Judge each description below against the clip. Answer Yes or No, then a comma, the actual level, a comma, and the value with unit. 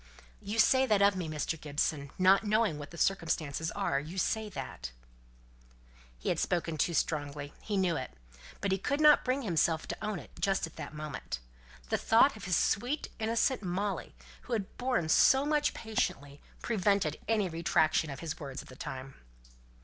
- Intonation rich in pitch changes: Yes, wide, 5.9 semitones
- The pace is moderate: Yes, average, 180 wpm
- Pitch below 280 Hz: Yes, medium, 185 Hz